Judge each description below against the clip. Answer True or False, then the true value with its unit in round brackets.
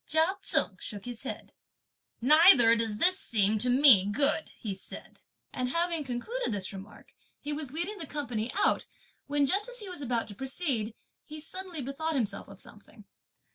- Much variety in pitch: True (6.2 semitones)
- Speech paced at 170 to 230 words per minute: True (175 wpm)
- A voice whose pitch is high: True (275 Hz)